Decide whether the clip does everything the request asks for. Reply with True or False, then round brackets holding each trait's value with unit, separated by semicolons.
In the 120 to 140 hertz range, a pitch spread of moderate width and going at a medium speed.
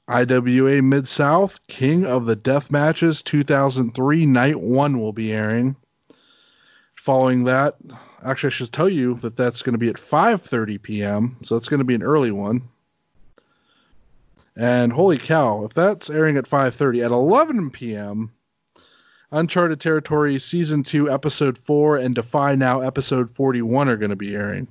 True (135 Hz; 3.8 semitones; 160 wpm)